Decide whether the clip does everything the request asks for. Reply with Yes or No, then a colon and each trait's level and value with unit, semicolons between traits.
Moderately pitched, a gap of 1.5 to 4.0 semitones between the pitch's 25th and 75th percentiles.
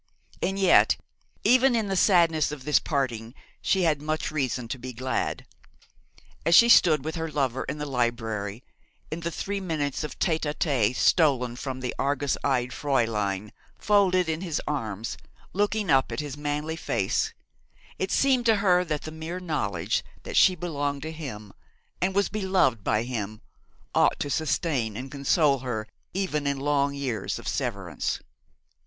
No: medium, 145 Hz; average, 5.2 semitones